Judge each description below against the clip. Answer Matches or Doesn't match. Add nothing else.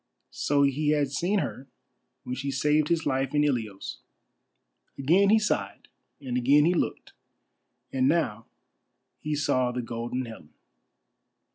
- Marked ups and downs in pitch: Doesn't match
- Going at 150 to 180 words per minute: Doesn't match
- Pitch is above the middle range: Doesn't match